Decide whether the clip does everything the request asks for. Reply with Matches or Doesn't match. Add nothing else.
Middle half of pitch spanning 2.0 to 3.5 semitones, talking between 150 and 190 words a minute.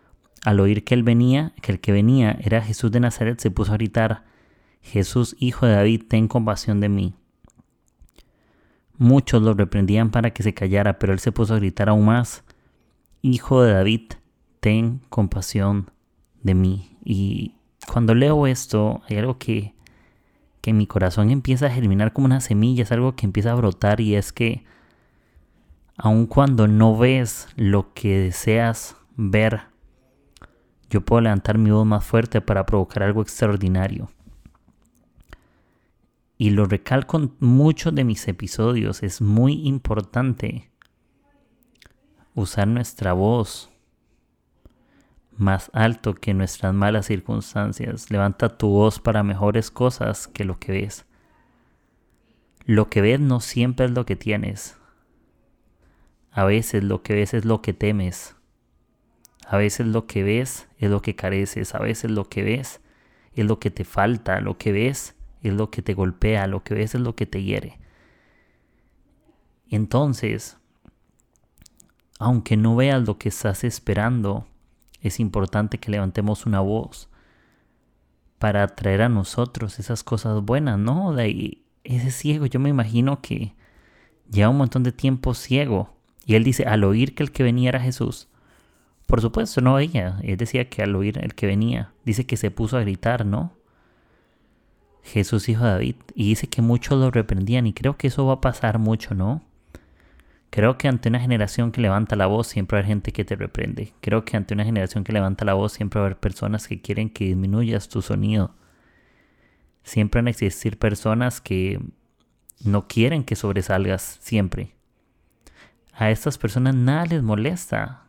Matches